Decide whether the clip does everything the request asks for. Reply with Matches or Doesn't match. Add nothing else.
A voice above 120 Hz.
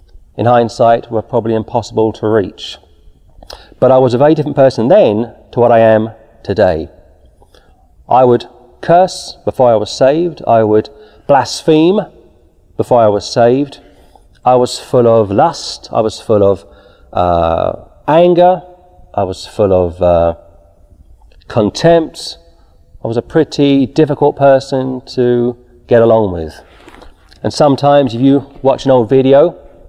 Doesn't match